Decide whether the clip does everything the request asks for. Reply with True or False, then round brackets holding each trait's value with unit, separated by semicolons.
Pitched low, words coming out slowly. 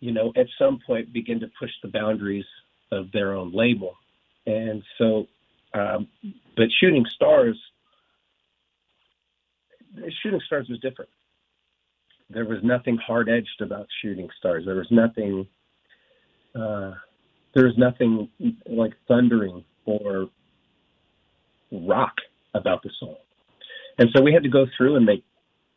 True (115 Hz; 130 wpm)